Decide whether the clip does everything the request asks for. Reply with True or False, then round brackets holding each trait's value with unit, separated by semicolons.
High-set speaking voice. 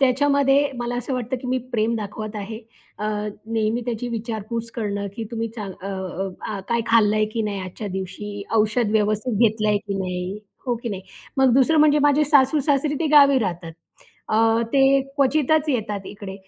True (225 Hz)